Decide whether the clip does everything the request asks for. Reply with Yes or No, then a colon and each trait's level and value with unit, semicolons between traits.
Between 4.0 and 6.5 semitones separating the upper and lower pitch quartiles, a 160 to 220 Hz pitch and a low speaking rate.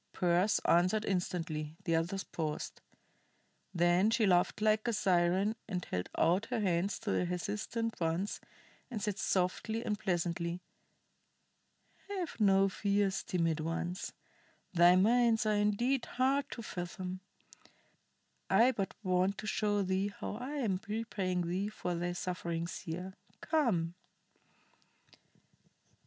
No: average, 3.6 semitones; high, 190 Hz; slow, 125 wpm